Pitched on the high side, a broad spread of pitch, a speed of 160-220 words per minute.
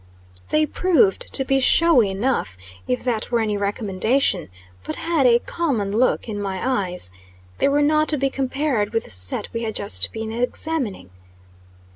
Yes: high, 235 Hz; wide, 5.7 semitones; average, 165 wpm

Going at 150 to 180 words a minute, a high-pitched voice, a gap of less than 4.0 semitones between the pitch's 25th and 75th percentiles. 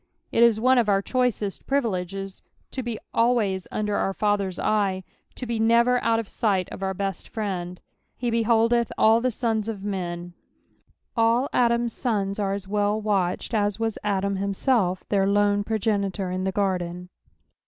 Yes: average, 160 wpm; high, 205 Hz; average, 2.9 semitones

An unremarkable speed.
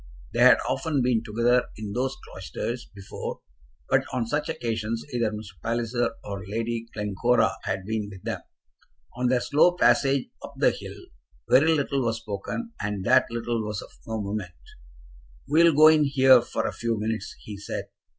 Yes: average, 170 wpm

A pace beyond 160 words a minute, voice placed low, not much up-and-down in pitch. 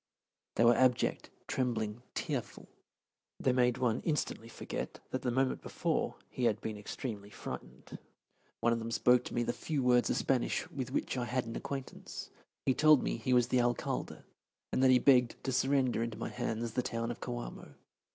Yes: average, 185 wpm; low, 125 Hz; narrow, 1.9 semitones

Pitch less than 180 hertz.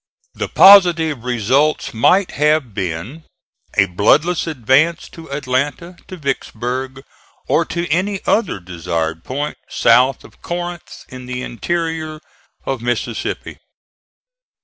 Yes: medium, 140 Hz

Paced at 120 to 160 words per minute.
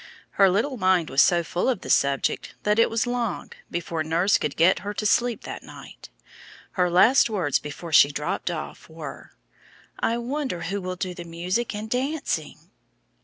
No: average, 175 wpm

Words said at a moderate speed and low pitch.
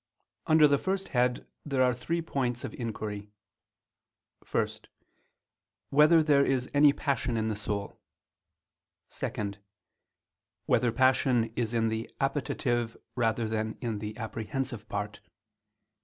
No: slow, 120 wpm; low, 120 Hz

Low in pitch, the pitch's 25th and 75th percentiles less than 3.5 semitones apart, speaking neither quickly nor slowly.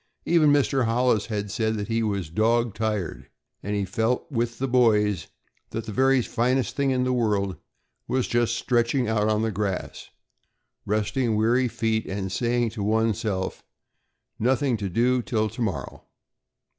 Yes: low, 115 Hz; average, 2.8 semitones; average, 155 wpm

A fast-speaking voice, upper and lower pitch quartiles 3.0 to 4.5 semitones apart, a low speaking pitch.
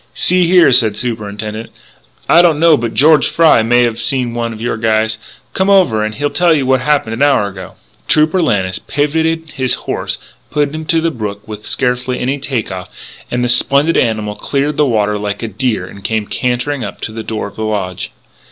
No: fast, 210 wpm; average, 5.3 semitones; low, 125 Hz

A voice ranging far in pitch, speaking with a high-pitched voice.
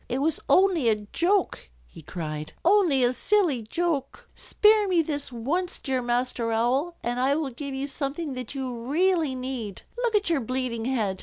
Yes: wide, 5.9 semitones; very high, 270 Hz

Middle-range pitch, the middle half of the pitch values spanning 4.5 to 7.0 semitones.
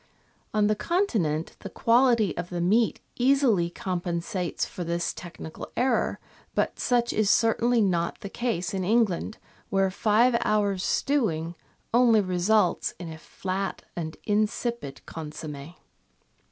No: high, 195 Hz; average, 5.1 semitones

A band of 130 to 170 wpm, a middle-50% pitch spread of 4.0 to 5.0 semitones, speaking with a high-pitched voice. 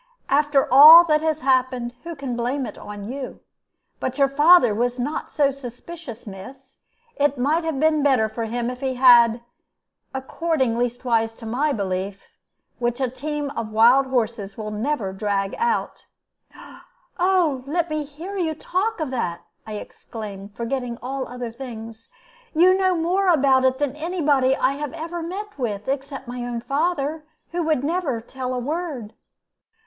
Yes: average, 165 wpm; average, 4.5 semitones; very high, 265 Hz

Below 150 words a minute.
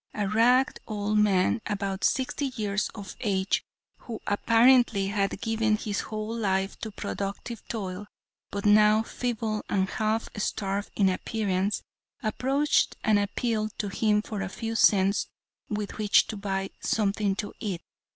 Yes: average, 140 wpm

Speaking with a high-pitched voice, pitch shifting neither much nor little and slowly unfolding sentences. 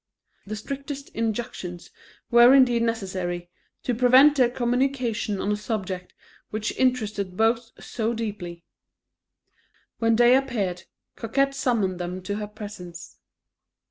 Yes: high, 225 Hz; average, 4.4 semitones; slow, 115 wpm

